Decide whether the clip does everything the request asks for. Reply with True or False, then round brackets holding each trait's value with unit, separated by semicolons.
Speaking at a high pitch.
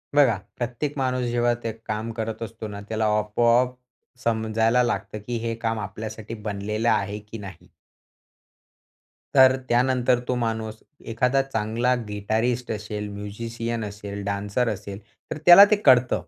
False (115 Hz)